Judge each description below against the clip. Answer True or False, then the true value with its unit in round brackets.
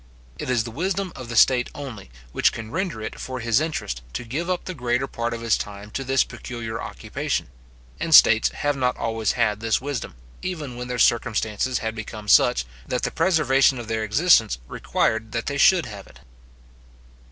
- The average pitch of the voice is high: False (120 Hz)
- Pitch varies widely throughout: False (3.9 semitones)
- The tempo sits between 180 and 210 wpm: True (190 wpm)